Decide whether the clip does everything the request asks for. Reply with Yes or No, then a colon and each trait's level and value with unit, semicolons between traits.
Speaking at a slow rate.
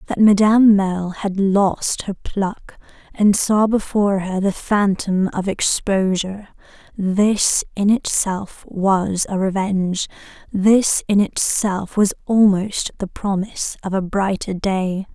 Yes: slow, 125 wpm